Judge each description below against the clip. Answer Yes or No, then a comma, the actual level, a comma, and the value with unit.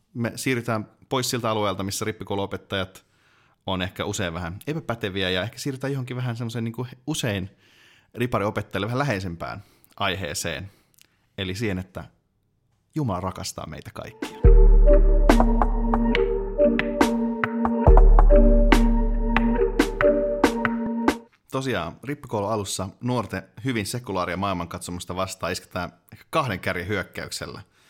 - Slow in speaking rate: Yes, slow, 90 wpm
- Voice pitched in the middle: No, low, 110 Hz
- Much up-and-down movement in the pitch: Yes, wide, 6.8 semitones